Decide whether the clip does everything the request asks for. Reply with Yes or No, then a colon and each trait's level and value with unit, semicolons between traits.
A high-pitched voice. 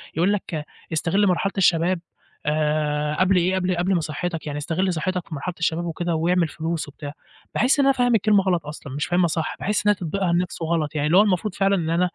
No: medium, 175 Hz